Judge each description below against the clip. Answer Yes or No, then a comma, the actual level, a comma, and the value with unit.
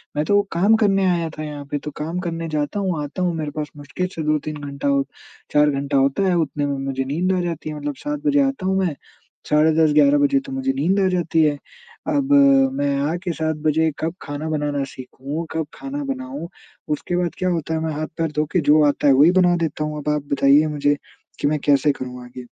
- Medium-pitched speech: Yes, medium, 155 Hz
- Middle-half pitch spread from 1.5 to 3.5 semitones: No, average, 3.9 semitones